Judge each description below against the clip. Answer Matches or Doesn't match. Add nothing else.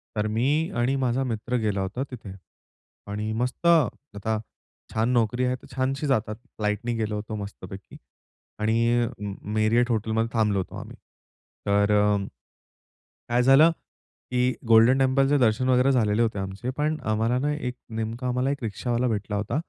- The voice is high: Doesn't match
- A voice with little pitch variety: Doesn't match